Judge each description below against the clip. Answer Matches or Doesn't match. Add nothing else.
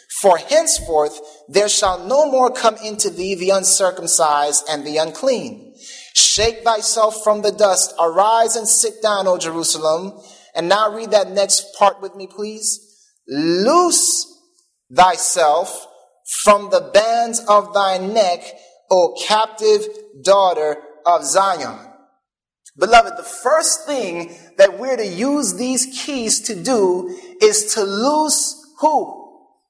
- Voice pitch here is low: Doesn't match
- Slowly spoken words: Matches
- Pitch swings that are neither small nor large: Doesn't match